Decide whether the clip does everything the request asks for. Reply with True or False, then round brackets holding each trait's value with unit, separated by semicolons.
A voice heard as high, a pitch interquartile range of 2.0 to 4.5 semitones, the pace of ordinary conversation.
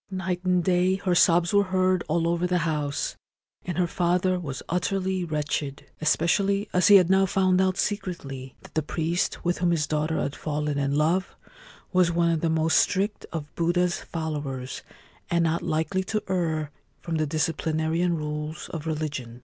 False (170 Hz; 2.9 semitones; 175 wpm)